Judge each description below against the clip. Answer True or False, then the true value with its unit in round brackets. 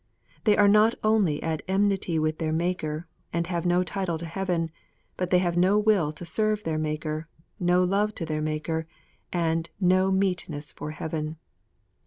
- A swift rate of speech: False (170 wpm)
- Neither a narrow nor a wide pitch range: True (3.3 semitones)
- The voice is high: False (175 Hz)